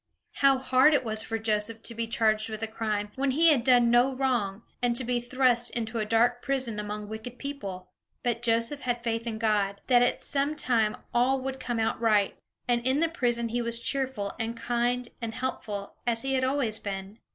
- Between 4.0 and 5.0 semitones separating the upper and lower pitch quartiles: No, average, 2.7 semitones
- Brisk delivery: Yes, fast, 210 wpm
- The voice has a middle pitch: No, high, 235 Hz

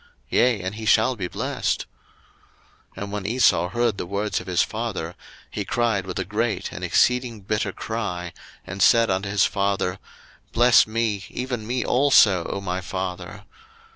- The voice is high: No, low, 105 Hz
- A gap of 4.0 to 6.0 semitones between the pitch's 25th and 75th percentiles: No, average, 3.6 semitones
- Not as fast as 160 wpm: No, average, 165 wpm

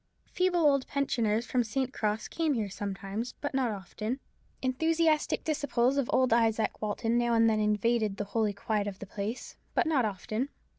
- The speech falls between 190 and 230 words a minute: No, average, 175 wpm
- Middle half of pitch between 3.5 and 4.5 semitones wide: Yes, average, 4.0 semitones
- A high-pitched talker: Yes, high, 230 Hz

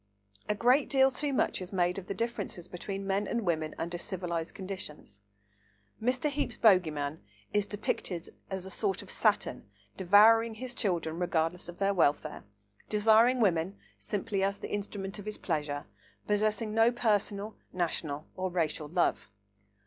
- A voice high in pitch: Yes, high, 195 Hz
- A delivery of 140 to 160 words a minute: Yes, average, 155 wpm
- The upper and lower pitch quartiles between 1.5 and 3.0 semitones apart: No, average, 3.9 semitones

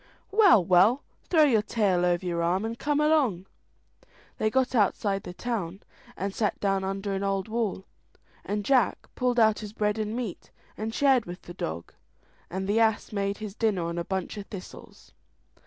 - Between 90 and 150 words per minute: No, average, 180 wpm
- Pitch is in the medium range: No, high, 205 Hz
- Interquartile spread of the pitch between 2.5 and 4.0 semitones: Yes, average, 3.2 semitones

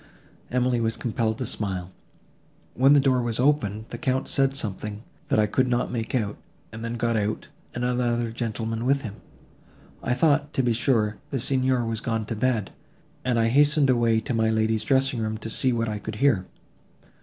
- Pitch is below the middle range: Yes, low, 115 Hz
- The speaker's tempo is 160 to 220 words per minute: Yes, average, 190 wpm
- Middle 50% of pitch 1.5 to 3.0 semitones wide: Yes, narrow, 2.6 semitones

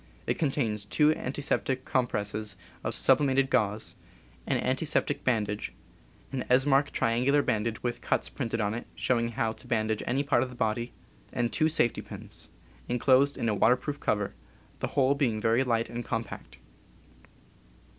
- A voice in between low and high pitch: No, low, 120 Hz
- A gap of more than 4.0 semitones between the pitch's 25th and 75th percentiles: No, average, 3.4 semitones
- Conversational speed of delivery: Yes, average, 155 wpm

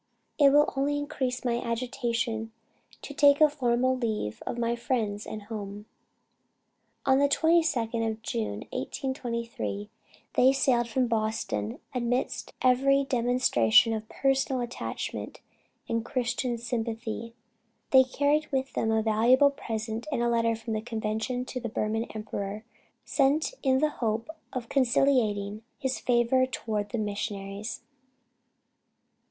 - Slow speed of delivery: Yes, slow, 130 wpm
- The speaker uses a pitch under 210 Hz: No, high, 235 Hz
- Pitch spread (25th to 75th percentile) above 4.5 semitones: No, average, 3.1 semitones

